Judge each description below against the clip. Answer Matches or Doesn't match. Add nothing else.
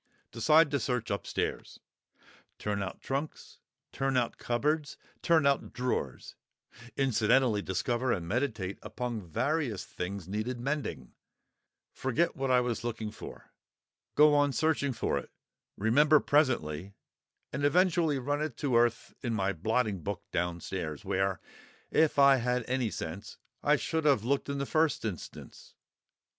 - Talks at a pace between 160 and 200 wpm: Doesn't match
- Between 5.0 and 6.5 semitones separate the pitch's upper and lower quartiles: Matches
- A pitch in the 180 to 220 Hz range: Doesn't match